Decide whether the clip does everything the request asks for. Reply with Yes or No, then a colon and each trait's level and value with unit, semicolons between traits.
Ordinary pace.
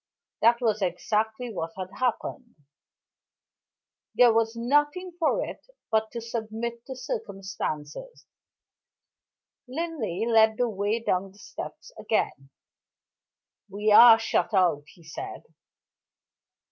No: slow, 110 wpm